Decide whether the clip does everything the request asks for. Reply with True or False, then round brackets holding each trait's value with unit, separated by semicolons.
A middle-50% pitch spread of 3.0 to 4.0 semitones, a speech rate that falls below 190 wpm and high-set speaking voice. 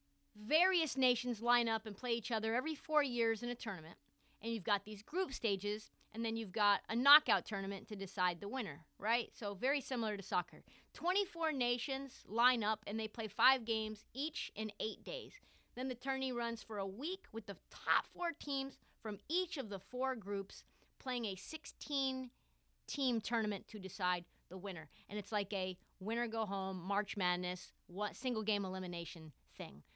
False (4.4 semitones; 180 wpm; 225 Hz)